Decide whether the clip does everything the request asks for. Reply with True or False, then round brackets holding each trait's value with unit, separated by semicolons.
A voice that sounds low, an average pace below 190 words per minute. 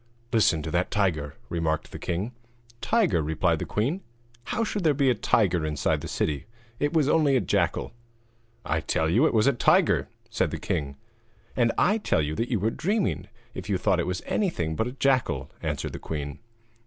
False (105 Hz; 195 wpm)